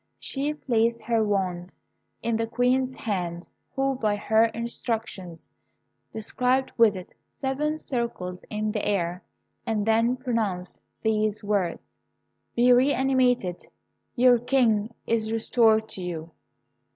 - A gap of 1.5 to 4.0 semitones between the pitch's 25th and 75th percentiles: Yes, average, 3.4 semitones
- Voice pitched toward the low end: No, high, 225 Hz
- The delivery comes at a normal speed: No, slow, 120 wpm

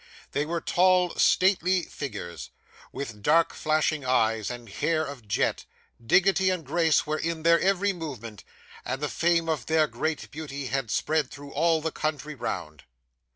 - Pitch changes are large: No, average, 4.5 semitones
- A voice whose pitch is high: No, medium, 155 Hz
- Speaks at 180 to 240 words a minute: No, average, 155 wpm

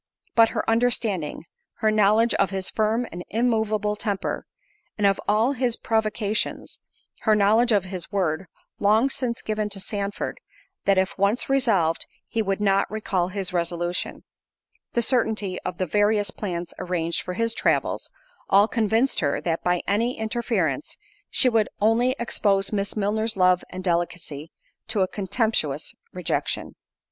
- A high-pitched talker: Yes, high, 205 Hz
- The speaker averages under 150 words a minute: Yes, average, 140 wpm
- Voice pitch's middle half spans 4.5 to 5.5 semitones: No, average, 3.3 semitones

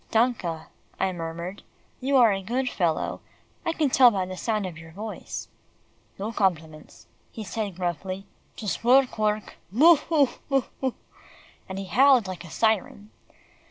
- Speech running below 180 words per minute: Yes, average, 155 wpm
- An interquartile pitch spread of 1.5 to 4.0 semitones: No, average, 5.1 semitones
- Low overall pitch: No, high, 210 Hz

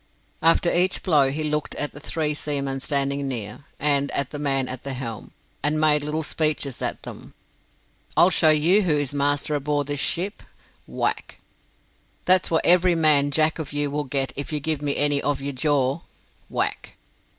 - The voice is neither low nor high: Yes, medium, 145 Hz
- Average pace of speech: Yes, average, 180 wpm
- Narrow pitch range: Yes, narrow, 1.9 semitones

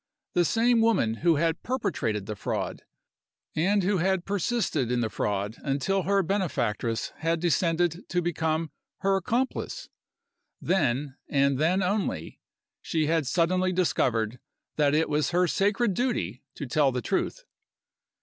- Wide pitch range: Yes, wide, 5.9 semitones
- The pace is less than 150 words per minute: Yes, average, 140 wpm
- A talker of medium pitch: Yes, medium, 165 Hz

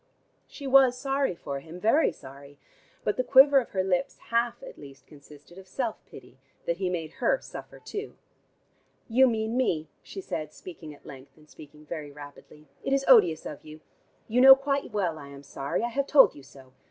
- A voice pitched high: No, medium, 180 Hz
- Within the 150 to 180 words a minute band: No, average, 195 wpm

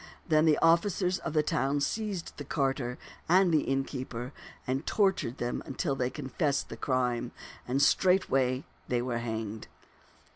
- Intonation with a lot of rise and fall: No, average, 4.8 semitones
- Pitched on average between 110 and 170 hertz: Yes, low, 135 Hz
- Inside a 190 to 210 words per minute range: No, average, 145 wpm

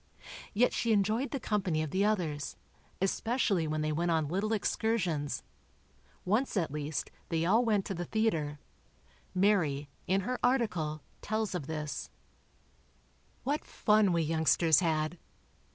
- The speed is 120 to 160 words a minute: Yes, slow, 135 wpm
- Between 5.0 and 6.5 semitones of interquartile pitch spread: Yes, wide, 5.6 semitones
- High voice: No, medium, 180 Hz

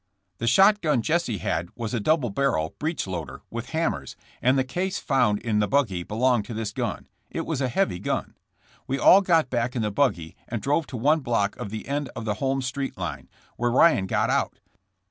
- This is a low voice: Yes, low, 125 Hz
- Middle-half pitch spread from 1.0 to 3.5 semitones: No, average, 5.1 semitones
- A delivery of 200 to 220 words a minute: Yes, fast, 205 wpm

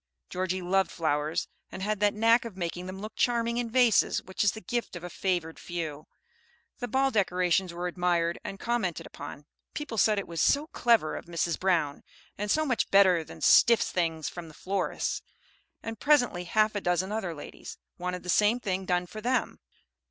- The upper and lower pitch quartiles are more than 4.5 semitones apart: No, average, 4.2 semitones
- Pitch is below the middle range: No, high, 190 Hz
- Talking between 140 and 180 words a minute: No, average, 190 wpm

